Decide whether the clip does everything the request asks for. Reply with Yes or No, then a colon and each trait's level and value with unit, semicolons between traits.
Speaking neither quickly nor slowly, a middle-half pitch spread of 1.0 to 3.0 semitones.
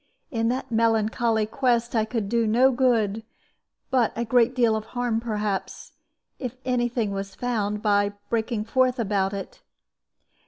Yes: average, 150 wpm; narrow, 2.6 semitones